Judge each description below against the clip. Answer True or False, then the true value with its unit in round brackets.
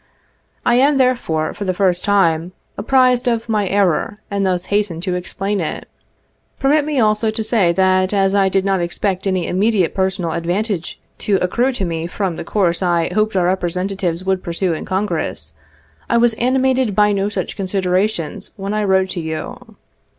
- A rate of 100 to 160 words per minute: False (175 wpm)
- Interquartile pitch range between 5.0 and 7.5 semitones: False (3.0 semitones)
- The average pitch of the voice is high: True (195 Hz)